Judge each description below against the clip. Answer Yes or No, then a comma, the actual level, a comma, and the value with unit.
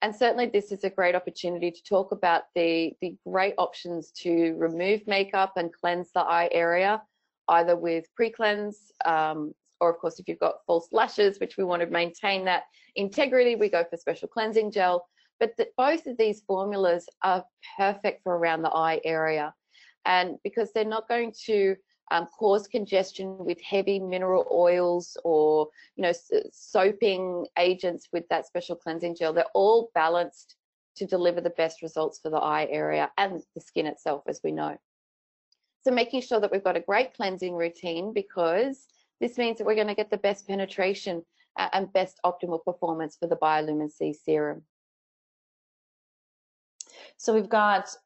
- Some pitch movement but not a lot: Yes, average, 3.4 semitones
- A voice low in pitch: No, medium, 180 Hz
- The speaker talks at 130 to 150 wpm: No, average, 170 wpm